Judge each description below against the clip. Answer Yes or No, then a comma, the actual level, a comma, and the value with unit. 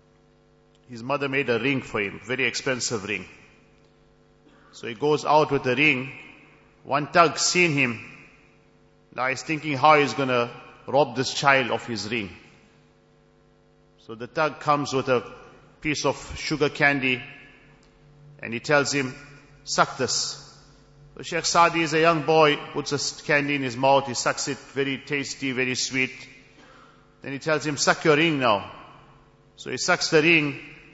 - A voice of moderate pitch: Yes, medium, 145 Hz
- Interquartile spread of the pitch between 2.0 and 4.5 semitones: Yes, narrow, 2.6 semitones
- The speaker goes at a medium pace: Yes, average, 160 wpm